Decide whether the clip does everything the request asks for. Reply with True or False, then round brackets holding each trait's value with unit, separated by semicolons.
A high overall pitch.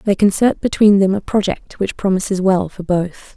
True (195 Hz)